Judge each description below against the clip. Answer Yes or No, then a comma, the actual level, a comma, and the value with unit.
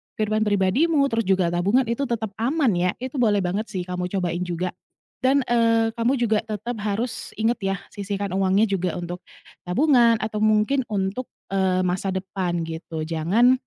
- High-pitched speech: Yes, high, 205 Hz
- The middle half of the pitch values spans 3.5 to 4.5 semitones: Yes, average, 4.2 semitones